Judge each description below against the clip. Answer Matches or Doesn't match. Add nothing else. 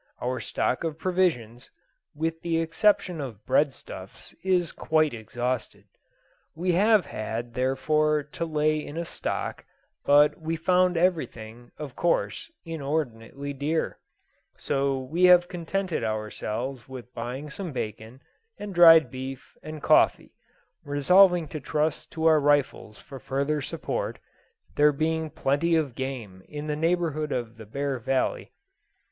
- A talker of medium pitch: Matches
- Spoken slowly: Matches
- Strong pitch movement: Doesn't match